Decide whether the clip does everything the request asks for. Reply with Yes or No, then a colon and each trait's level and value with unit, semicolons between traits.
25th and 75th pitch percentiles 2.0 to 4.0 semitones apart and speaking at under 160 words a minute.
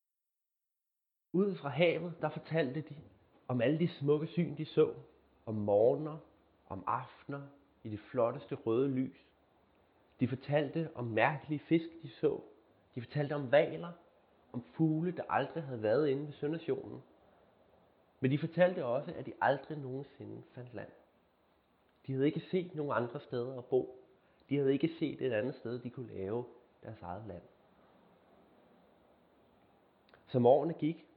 No: average, 4.6 semitones; average, 150 wpm